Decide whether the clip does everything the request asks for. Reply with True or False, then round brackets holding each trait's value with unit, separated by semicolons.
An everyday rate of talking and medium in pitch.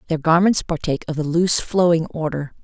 True (180 wpm; 165 Hz)